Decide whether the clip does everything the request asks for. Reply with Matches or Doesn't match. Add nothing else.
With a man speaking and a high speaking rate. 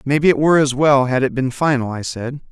Matches